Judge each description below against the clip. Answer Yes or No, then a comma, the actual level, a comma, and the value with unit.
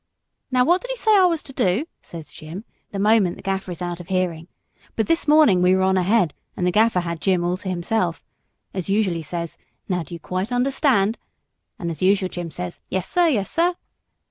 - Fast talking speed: Yes, fast, 220 wpm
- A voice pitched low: No, high, 190 Hz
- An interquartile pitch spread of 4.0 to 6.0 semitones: Yes, average, 4.8 semitones